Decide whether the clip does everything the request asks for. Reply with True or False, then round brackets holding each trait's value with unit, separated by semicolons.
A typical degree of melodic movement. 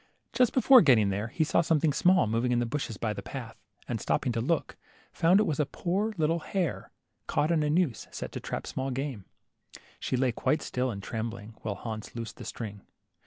False (6.2 semitones)